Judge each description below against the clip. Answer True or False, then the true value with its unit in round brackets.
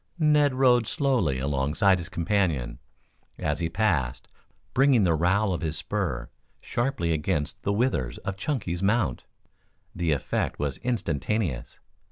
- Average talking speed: False (130 wpm)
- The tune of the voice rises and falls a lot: True (7.3 semitones)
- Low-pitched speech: True (90 Hz)